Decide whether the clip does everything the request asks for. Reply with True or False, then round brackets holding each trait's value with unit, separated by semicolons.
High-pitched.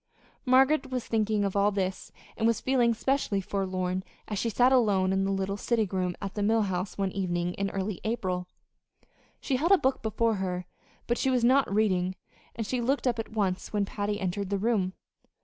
True (205 Hz)